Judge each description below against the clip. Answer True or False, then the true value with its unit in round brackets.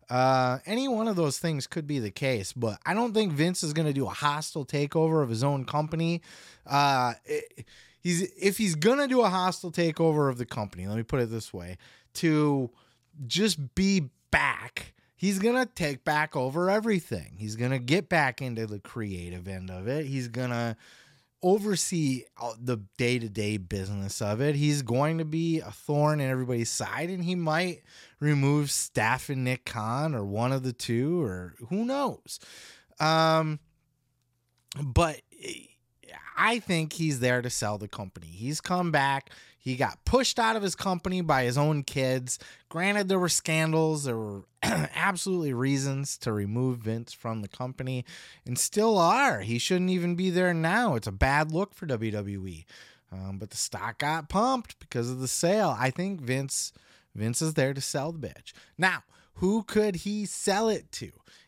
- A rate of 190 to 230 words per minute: False (180 wpm)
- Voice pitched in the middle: True (145 Hz)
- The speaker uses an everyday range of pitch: False (6.1 semitones)